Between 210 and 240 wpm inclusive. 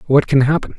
Yes: fast, 230 wpm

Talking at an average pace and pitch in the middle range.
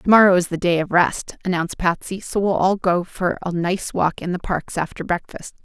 No: fast, 225 wpm; medium, 180 Hz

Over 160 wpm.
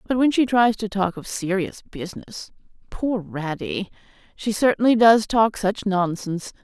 No: average, 145 wpm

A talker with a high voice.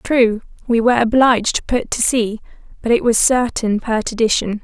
Yes: high, 230 Hz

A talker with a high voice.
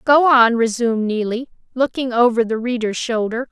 Yes: high, 235 Hz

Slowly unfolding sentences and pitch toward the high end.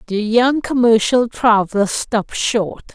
Yes: slow, 120 wpm; high, 225 Hz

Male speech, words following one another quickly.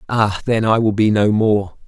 Yes: male; fast, 225 wpm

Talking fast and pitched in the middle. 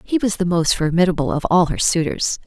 Yes: fast, 220 wpm; medium, 175 Hz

